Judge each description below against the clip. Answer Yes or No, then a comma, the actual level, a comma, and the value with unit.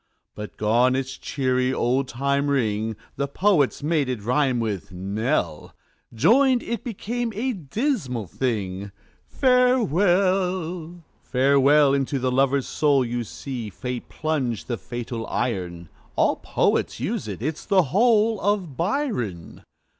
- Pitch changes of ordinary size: No, wide, 7.5 semitones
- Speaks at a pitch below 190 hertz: Yes, low, 135 Hz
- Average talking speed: No, slow, 125 wpm